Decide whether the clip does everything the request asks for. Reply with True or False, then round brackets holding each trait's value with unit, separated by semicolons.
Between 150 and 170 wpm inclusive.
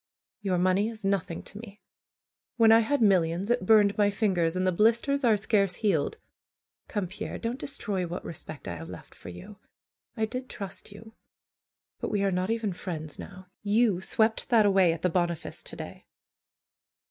False (180 wpm)